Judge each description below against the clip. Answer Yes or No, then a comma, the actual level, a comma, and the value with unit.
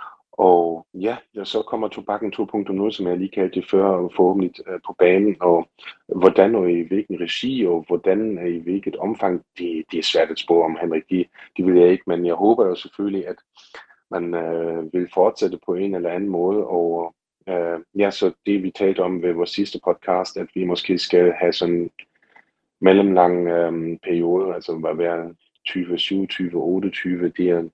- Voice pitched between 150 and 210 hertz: No, very low, 90 Hz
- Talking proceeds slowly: No, average, 185 wpm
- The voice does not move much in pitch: Yes, narrow, 1.8 semitones